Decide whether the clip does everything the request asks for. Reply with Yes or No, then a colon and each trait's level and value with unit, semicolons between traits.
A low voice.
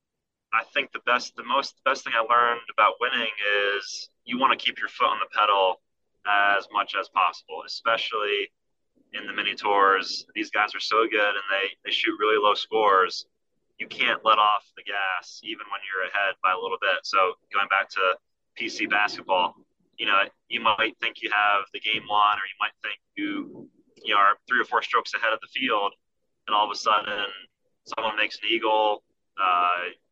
Yes: low, 115 Hz